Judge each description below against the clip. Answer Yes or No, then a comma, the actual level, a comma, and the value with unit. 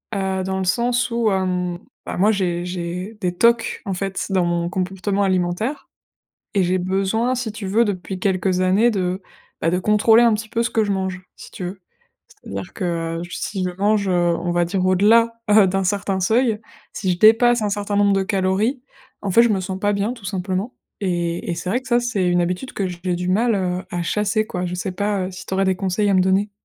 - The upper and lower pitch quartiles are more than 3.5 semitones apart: No, average, 2.8 semitones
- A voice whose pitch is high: Yes, high, 195 Hz